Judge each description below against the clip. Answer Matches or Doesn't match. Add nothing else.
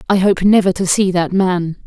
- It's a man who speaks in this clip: Doesn't match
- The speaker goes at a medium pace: Doesn't match